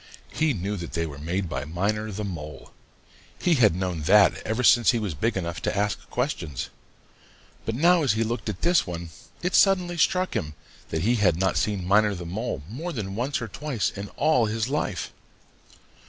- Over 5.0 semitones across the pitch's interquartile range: Yes, wide, 5.6 semitones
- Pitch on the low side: Yes, low, 105 Hz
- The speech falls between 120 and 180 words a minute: No, average, 200 wpm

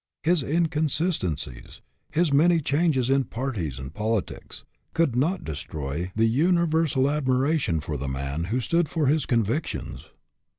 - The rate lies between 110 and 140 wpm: Yes, slow, 135 wpm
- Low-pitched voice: Yes, low, 130 Hz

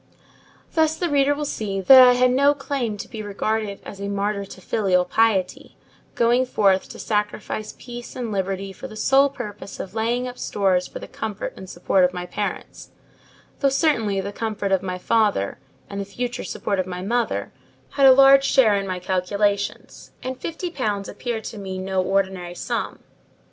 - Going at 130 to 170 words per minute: No, average, 185 wpm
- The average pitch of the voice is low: No, high, 210 Hz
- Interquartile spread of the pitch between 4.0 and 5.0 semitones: Yes, average, 4.4 semitones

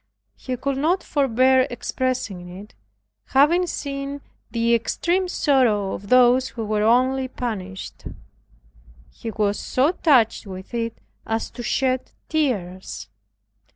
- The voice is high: Yes, very high, 250 Hz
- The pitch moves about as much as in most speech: Yes, average, 4.1 semitones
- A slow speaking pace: Yes, slow, 120 wpm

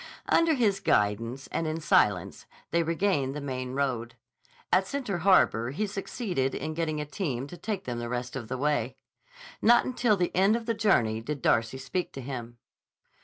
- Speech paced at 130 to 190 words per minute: Yes, average, 180 wpm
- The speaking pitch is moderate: Yes, medium, 145 Hz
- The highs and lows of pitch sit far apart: Yes, wide, 7.8 semitones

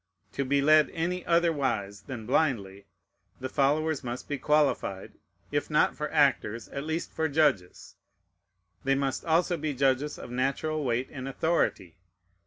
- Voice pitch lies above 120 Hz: Yes, medium, 140 Hz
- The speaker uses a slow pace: No, average, 145 wpm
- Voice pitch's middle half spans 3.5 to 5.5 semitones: Yes, average, 4.1 semitones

